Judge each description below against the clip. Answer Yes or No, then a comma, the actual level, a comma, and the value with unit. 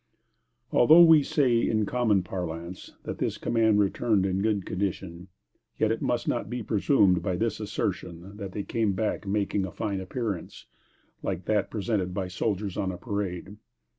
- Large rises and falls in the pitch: No, average, 2.9 semitones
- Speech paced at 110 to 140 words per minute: No, average, 165 wpm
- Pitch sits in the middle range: No, low, 100 Hz